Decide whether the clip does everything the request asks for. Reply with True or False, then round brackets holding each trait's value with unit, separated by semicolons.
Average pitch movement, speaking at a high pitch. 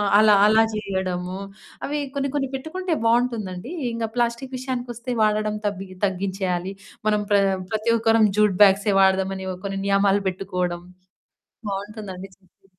True (3.3 semitones; 205 Hz)